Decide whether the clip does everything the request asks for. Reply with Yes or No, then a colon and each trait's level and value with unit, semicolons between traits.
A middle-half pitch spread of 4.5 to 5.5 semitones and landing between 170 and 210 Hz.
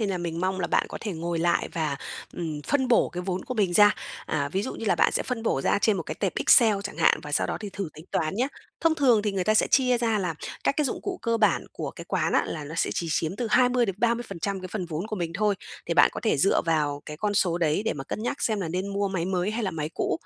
Yes: average, 4.9 semitones; high, 195 Hz